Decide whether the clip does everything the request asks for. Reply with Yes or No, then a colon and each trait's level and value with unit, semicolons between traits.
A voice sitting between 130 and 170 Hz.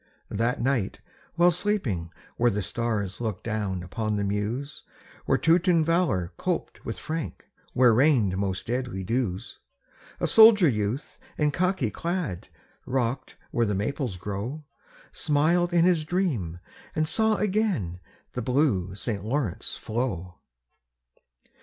No: low, 120 Hz